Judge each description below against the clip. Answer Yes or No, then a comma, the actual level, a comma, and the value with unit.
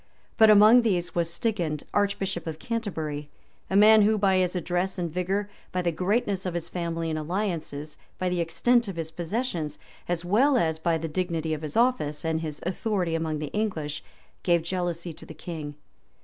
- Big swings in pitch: No, average, 4.0 semitones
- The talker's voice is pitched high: No, medium, 175 Hz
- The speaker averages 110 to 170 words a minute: No, average, 185 wpm